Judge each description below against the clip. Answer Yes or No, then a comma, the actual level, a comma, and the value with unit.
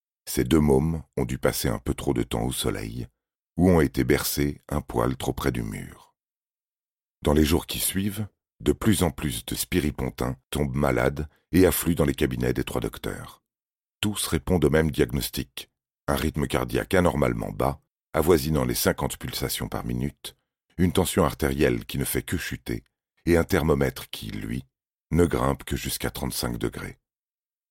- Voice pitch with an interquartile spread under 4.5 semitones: Yes, average, 4.1 semitones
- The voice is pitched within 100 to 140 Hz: No, very low, 75 Hz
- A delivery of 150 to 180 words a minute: Yes, average, 170 wpm